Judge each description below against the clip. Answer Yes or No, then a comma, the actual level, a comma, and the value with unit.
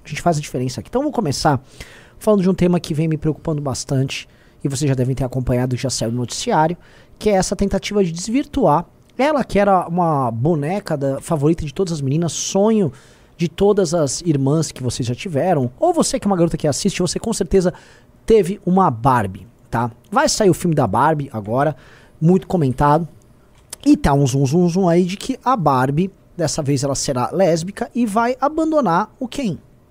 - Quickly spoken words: Yes, fast, 200 wpm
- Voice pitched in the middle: Yes, medium, 165 Hz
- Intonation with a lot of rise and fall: Yes, wide, 6.4 semitones